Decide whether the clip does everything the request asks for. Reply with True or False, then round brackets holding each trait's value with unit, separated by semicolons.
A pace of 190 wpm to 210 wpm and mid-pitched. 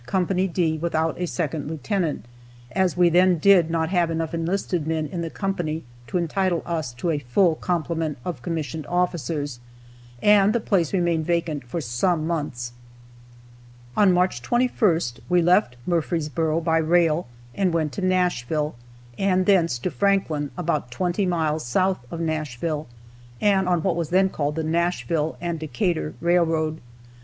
False (150 wpm; 165 Hz)